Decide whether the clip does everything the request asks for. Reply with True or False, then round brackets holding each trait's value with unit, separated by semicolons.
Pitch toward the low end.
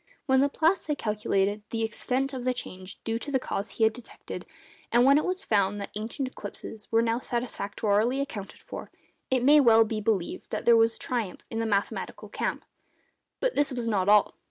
False (230 Hz)